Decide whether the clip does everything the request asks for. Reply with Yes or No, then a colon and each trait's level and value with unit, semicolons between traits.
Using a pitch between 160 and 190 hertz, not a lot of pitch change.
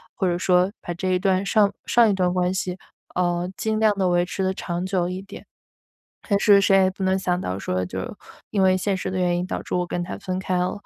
Yes: medium, 185 Hz; narrow, 1.5 semitones